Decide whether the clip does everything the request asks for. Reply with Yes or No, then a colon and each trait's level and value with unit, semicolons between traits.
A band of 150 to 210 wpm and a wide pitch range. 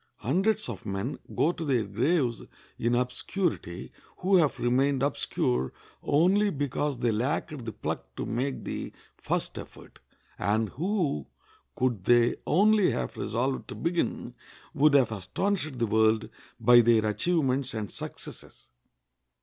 No: slow, 135 wpm; wide, 6.0 semitones